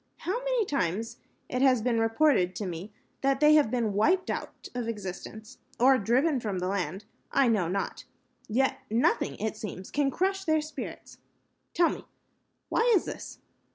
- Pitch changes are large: Yes, wide, 6.2 semitones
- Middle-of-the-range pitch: No, high, 240 Hz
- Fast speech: No, average, 165 wpm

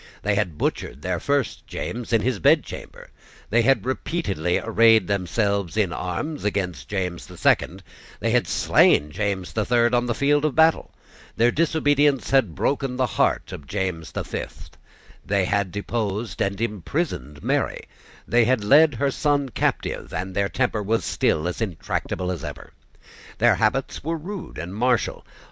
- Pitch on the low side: Yes, low, 110 Hz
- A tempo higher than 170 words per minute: No, average, 160 wpm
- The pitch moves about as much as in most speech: No, wide, 5.8 semitones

